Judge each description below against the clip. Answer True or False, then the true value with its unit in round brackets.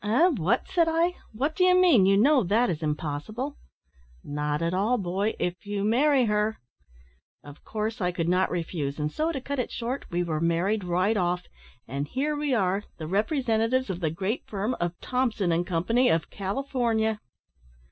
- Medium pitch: False (210 Hz)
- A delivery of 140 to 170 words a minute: False (180 wpm)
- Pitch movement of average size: False (6.4 semitones)